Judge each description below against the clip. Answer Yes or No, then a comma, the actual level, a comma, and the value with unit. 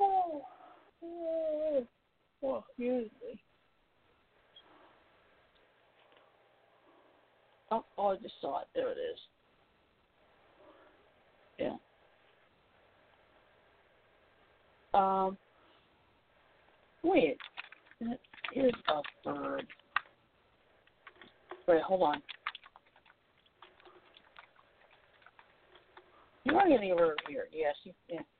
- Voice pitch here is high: Yes, very high, 280 Hz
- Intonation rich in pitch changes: Yes, wide, 7.9 semitones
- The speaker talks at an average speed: No, slow, 70 wpm